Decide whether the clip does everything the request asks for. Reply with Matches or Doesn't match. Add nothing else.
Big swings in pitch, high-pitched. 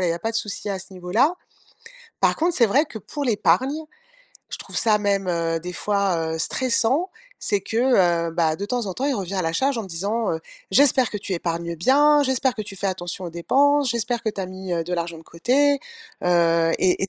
Matches